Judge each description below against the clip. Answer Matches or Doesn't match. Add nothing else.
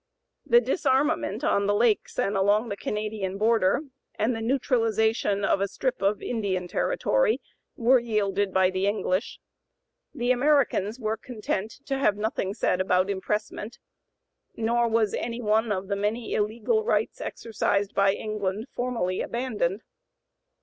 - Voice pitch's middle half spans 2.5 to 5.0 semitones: Matches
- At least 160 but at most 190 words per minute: Doesn't match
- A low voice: Doesn't match